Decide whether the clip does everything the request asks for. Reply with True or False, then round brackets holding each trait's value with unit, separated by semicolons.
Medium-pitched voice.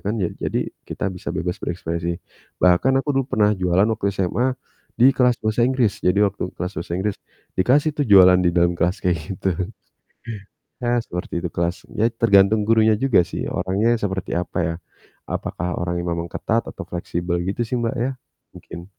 False (95 Hz)